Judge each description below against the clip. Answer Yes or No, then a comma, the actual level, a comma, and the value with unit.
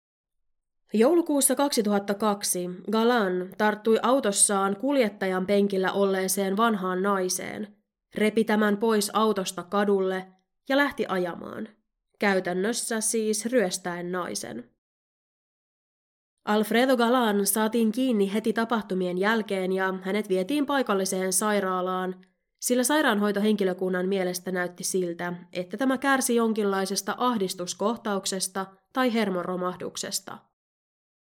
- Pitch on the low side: No, high, 200 Hz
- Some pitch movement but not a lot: Yes, average, 3.1 semitones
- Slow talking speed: Yes, slow, 90 wpm